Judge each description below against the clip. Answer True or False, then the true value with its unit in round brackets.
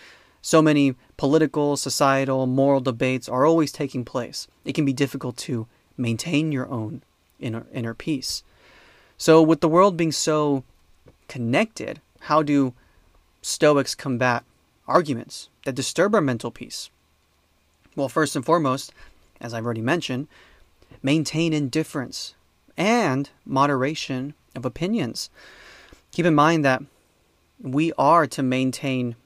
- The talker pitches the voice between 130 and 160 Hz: True (135 Hz)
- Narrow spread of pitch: False (3.7 semitones)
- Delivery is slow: True (125 wpm)